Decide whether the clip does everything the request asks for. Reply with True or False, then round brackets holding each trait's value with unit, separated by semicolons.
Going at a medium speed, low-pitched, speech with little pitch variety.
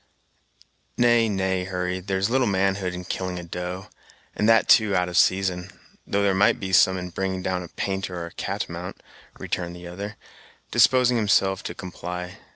True (170 wpm; 95 Hz; 1.9 semitones)